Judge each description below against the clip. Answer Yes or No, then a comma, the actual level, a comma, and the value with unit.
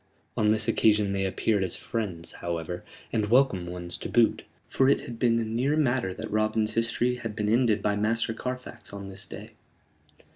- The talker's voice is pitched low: Yes, low, 110 Hz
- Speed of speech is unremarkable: Yes, average, 185 wpm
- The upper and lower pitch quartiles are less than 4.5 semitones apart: Yes, average, 3.2 semitones